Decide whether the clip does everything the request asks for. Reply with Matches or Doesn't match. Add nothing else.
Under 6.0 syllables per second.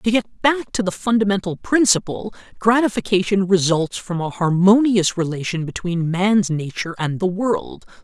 Matches